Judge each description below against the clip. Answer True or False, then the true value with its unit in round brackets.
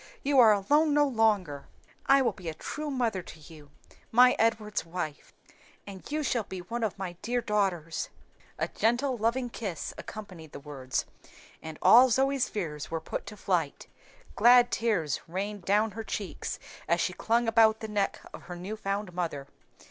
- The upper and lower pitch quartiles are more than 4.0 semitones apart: True (5.2 semitones)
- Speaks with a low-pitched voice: False (210 Hz)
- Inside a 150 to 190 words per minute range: True (170 wpm)